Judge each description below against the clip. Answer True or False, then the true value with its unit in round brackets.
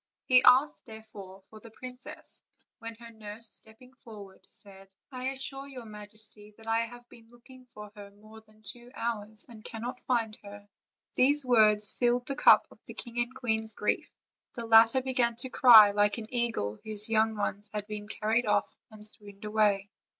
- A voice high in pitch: True (220 Hz)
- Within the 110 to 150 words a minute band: False (180 wpm)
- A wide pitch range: False (2.4 semitones)